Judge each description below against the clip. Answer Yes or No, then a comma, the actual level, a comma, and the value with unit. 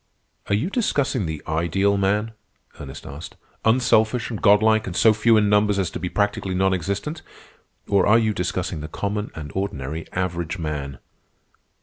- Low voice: Yes, low, 100 Hz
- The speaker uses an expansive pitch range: No, average, 3.9 semitones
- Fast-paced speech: No, average, 160 wpm